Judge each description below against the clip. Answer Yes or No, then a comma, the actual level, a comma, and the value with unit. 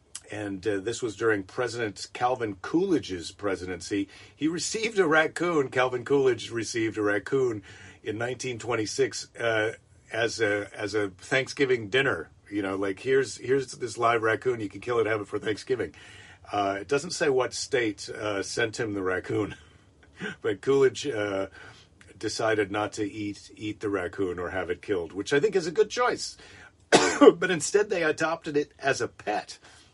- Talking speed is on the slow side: No, average, 165 wpm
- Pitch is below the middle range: Yes, low, 125 Hz